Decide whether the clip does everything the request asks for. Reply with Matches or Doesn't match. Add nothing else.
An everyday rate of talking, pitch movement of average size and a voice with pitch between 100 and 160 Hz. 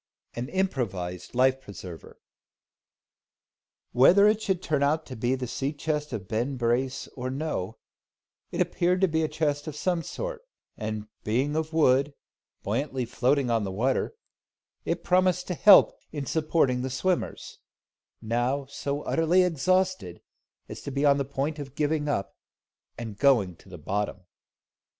Matches